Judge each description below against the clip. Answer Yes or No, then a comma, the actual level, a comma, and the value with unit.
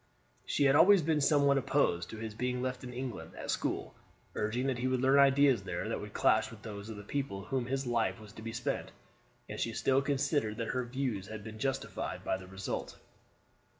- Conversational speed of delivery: No, fast, 220 wpm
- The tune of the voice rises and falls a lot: No, average, 3.9 semitones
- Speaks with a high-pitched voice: No, low, 125 Hz